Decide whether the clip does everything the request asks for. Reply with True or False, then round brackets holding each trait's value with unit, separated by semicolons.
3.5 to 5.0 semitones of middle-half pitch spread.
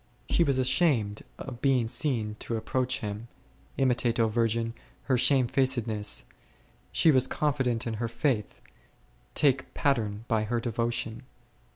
False (2.7 semitones)